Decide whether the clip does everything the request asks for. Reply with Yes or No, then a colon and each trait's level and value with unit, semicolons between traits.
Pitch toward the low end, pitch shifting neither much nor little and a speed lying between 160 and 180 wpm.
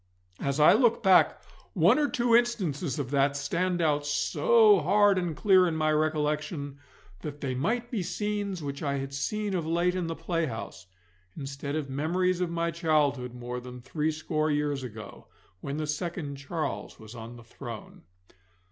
No: medium, 155 Hz; average, 4.6 semitones; average, 165 wpm